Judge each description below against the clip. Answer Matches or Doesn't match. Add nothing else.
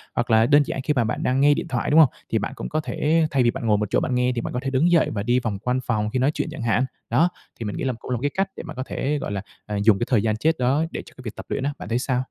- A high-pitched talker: Doesn't match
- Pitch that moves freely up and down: Doesn't match